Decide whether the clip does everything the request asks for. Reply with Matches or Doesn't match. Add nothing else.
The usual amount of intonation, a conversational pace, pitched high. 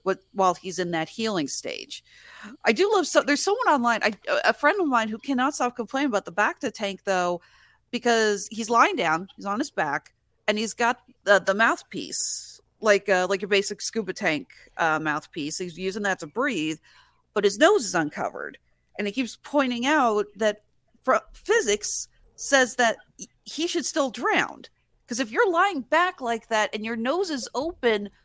Doesn't match